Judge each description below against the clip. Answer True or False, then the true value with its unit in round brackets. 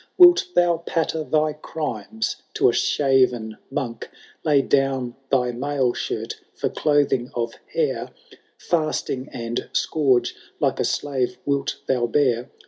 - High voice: False (135 Hz)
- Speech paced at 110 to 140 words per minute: True (135 wpm)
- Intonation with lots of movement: False (3.8 semitones)